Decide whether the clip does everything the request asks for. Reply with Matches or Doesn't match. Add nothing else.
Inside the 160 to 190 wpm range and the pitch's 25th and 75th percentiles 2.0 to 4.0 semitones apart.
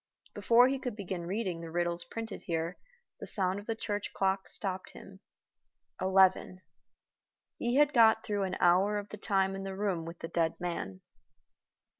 Matches